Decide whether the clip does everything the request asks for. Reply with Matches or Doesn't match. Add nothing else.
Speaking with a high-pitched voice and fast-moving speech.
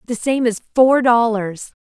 Doesn't match